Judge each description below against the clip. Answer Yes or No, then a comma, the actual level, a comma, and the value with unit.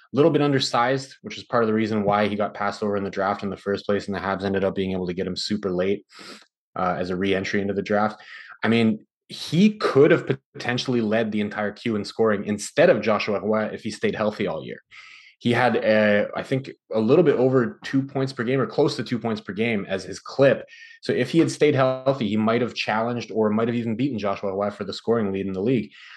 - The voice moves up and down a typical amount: Yes, average, 3.7 semitones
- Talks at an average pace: No, fast, 250 wpm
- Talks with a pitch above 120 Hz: No, low, 110 Hz